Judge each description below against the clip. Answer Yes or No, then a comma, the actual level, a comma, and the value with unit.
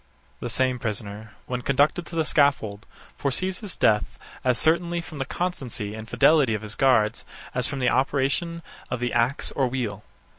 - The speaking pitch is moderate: No, low, 130 Hz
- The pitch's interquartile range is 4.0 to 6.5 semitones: Yes, average, 5.1 semitones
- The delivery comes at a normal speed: Yes, average, 175 wpm